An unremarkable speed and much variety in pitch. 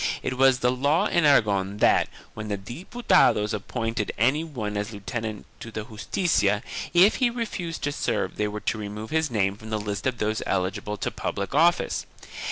Yes: average, 180 wpm; wide, 5.9 semitones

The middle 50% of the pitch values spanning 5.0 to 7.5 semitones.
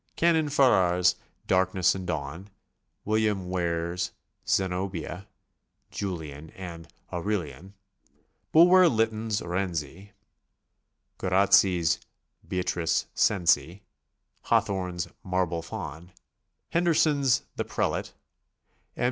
No: average, 3.3 semitones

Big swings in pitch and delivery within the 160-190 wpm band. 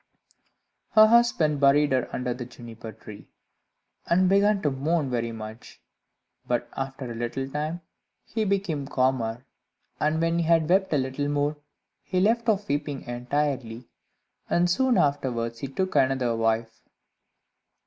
No: wide, 5.8 semitones; average, 140 wpm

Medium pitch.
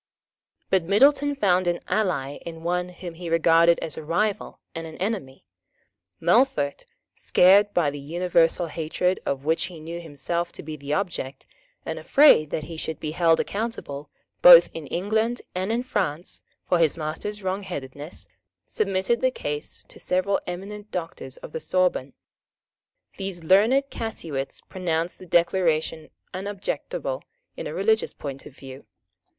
Yes: medium, 175 Hz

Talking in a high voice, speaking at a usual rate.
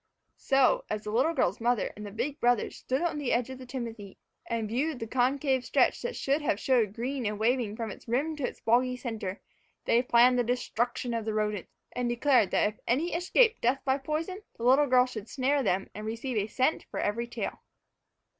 No: high, 245 Hz; fast, 210 wpm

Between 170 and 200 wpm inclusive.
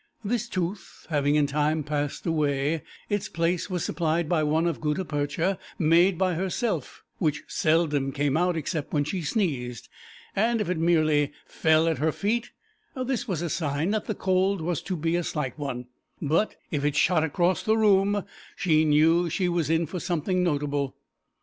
Yes: average, 175 wpm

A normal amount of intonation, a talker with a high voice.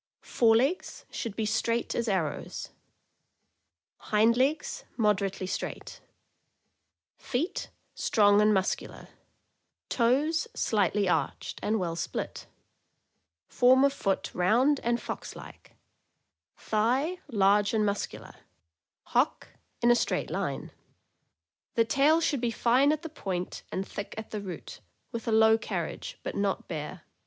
Yes: average, 4.2 semitones; high, 225 Hz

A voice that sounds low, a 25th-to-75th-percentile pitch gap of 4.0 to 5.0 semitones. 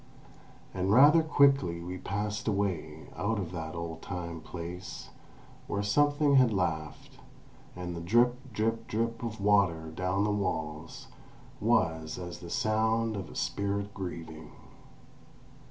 Yes: very low, 95 Hz; average, 4.7 semitones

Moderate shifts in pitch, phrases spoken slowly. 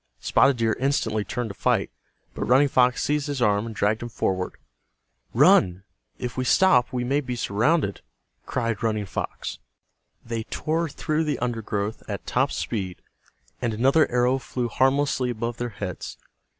No: average, 3.6 semitones; average, 155 wpm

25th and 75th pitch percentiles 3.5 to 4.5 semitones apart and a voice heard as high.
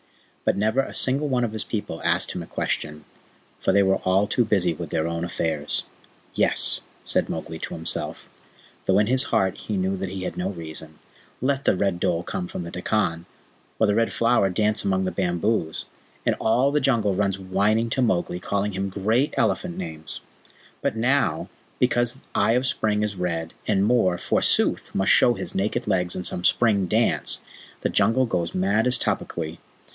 No: average, 4.2 semitones; low, 100 Hz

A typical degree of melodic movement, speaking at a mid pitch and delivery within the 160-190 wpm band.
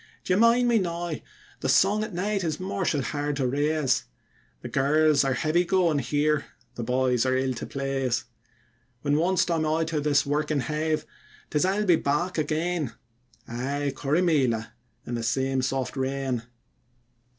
No: average, 4.2 semitones; medium, 150 Hz; average, 150 wpm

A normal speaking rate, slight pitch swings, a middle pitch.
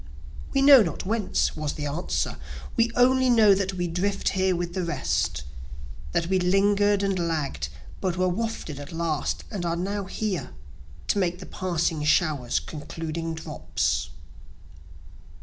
No: average, 150 wpm; average, 3.7 semitones; medium, 180 Hz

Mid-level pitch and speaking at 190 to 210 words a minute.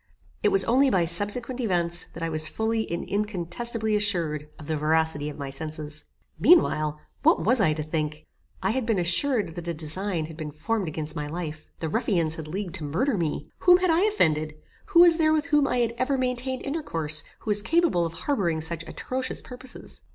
Yes: medium, 175 Hz; average, 200 wpm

